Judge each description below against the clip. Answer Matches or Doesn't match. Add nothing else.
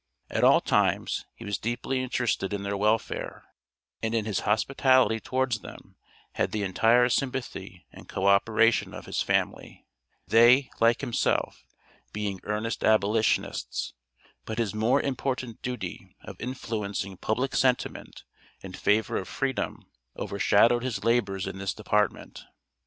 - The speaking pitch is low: Matches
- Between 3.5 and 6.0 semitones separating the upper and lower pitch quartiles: Doesn't match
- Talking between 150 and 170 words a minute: Doesn't match